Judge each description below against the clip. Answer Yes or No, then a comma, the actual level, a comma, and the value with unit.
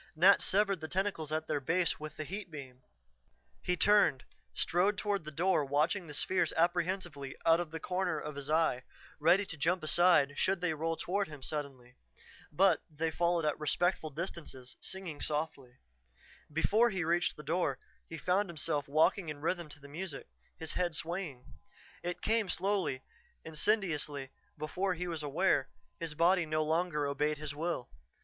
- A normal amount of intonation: Yes, average, 3.3 semitones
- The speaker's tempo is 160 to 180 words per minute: Yes, average, 165 wpm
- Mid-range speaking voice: Yes, medium, 160 Hz